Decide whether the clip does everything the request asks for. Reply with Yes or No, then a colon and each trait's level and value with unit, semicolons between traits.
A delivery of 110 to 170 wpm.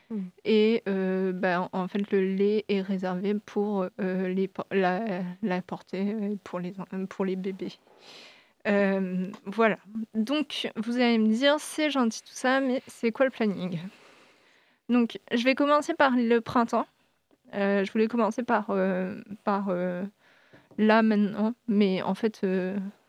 Yes: average, 150 wpm